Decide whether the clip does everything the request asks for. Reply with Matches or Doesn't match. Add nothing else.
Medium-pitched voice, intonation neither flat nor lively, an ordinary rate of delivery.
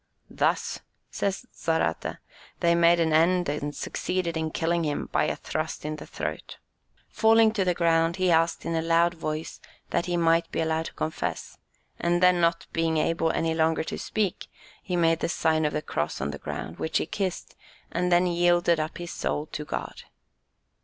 Doesn't match